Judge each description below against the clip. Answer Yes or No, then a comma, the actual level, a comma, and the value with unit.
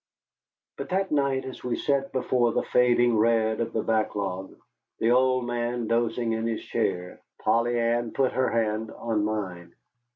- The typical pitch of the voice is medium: No, low, 115 Hz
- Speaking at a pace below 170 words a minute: Yes, average, 160 wpm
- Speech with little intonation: Yes, narrow, 2.1 semitones